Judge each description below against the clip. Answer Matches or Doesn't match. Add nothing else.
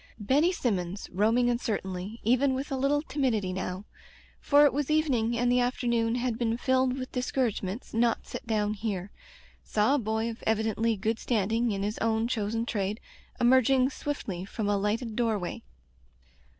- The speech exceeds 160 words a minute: Matches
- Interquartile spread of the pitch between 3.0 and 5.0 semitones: Matches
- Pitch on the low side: Doesn't match